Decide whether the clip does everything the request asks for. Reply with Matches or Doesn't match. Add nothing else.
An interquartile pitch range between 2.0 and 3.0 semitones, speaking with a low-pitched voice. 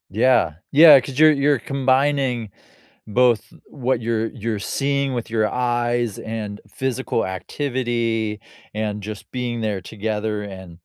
Doesn't match